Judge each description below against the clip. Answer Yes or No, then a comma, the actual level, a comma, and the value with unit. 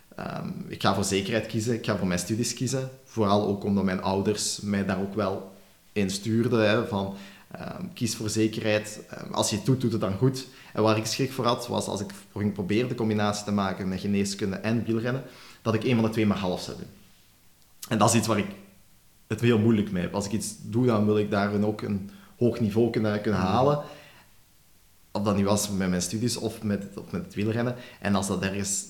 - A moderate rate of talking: No, fast, 225 wpm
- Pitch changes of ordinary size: Yes, average, 3.0 semitones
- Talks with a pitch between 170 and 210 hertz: No, low, 105 Hz